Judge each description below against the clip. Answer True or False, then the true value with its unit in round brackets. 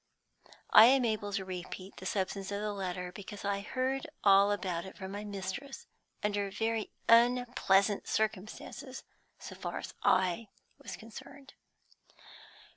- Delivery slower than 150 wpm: True (135 wpm)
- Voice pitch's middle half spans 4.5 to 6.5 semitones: False (2.9 semitones)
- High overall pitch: True (205 Hz)